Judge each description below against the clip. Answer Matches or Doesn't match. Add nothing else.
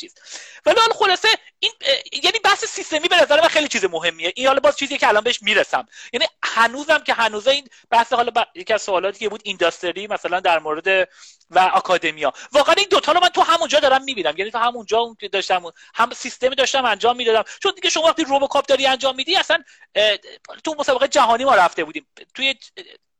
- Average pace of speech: Doesn't match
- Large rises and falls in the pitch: Matches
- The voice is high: Matches